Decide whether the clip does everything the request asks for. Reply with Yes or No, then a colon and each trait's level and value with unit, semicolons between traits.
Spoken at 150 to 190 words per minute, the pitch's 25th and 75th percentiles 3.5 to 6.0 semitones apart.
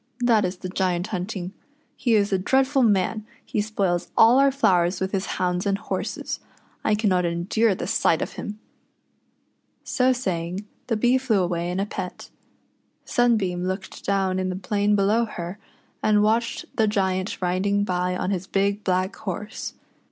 No: average, 165 wpm; average, 3.0 semitones